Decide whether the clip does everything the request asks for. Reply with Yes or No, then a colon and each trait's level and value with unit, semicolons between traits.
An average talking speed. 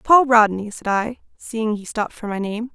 No: fast, 220 wpm